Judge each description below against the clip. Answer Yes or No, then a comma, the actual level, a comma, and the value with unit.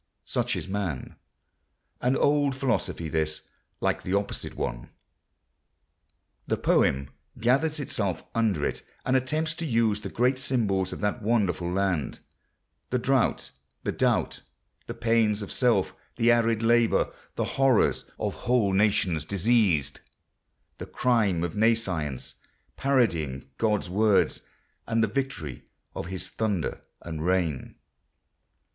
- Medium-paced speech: No, slow, 125 wpm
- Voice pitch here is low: Yes, low, 105 Hz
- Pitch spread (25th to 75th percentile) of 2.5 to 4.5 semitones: No, average, 5.2 semitones